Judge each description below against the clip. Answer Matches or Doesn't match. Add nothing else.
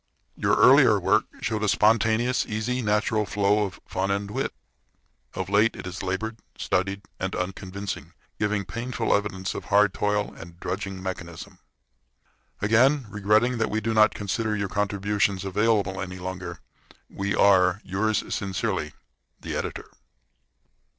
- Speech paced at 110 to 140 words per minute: Matches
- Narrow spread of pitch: Matches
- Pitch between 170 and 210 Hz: Doesn't match